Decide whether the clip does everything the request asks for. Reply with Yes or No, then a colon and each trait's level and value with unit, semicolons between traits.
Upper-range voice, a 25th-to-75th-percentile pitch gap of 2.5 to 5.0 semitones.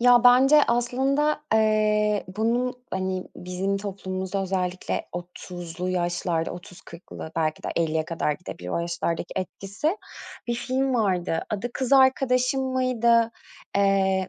No: high, 195 Hz; wide, 5.5 semitones